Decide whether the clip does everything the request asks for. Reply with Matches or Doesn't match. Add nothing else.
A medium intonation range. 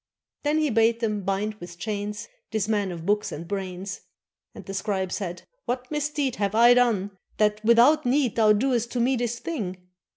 Matches